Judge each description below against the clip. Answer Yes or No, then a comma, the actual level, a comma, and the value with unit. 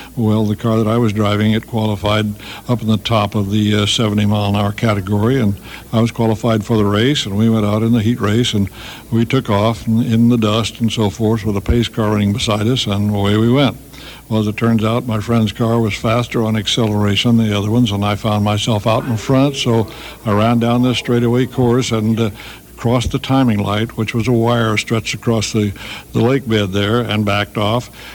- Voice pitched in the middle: No, low, 110 Hz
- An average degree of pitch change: No, narrow, 2.1 semitones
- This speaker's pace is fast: Yes, fast, 230 wpm